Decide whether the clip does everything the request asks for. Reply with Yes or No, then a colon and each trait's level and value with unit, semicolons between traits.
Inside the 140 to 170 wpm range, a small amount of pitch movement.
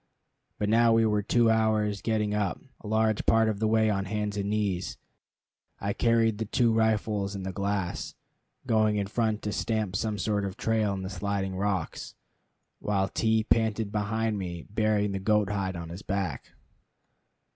No: average, 180 wpm; narrow, 2.0 semitones